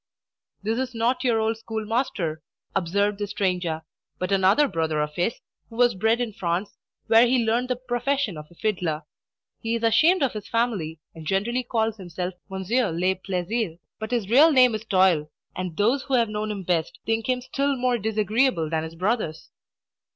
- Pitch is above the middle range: Yes, high, 215 Hz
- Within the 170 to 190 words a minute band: Yes, average, 180 wpm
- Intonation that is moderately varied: Yes, average, 4.9 semitones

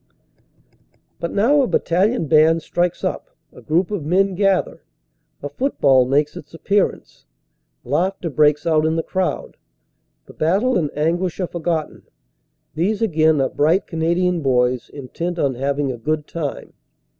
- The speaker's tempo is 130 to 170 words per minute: Yes, average, 145 wpm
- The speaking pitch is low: No, medium, 165 Hz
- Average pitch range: Yes, average, 3.8 semitones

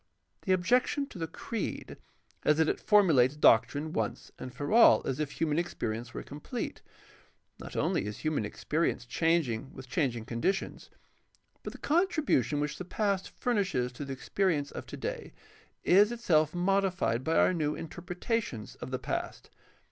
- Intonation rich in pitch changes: Yes, wide, 6.7 semitones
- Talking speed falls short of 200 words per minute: Yes, average, 155 wpm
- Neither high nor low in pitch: Yes, medium, 160 Hz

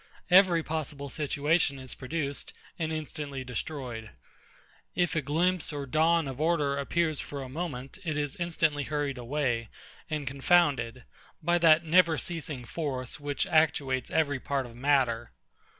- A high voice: No, medium, 145 Hz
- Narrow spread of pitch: No, average, 3.3 semitones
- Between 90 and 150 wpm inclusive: Yes, average, 140 wpm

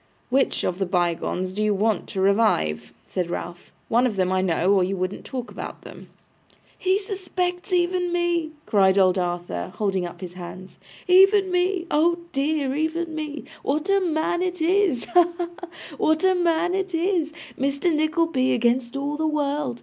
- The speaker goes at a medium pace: Yes, average, 175 wpm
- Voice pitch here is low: No, very high, 295 Hz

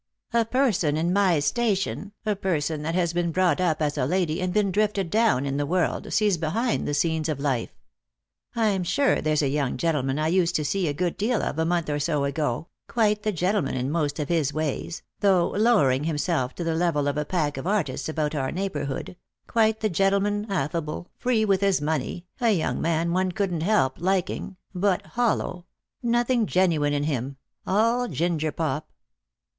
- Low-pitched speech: No, medium, 170 Hz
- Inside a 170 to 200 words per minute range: Yes, average, 195 wpm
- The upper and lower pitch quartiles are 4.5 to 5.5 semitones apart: Yes, average, 4.9 semitones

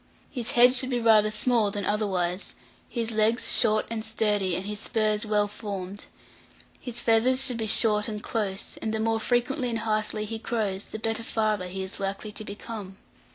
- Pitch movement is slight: Yes, narrow, 1.7 semitones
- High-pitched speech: Yes, high, 215 Hz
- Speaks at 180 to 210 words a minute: Yes, average, 185 wpm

